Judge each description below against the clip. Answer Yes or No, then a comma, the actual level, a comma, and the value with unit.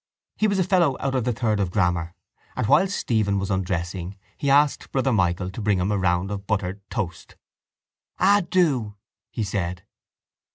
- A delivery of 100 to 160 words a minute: No, average, 175 wpm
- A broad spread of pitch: Yes, wide, 6.3 semitones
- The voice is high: No, low, 105 Hz